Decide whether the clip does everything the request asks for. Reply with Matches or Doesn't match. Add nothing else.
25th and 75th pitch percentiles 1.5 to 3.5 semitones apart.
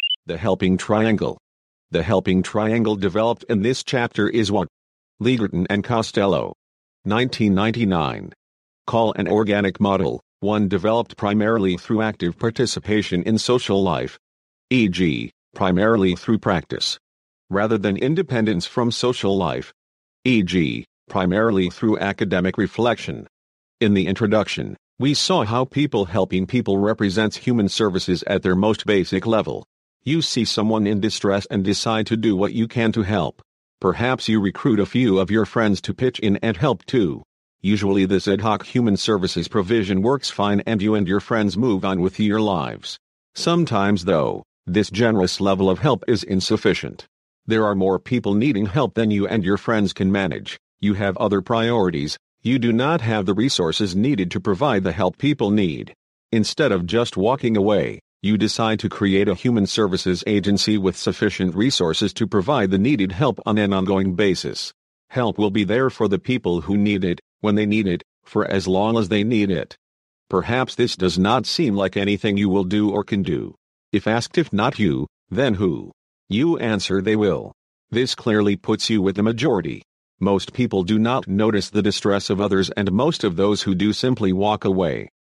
Matches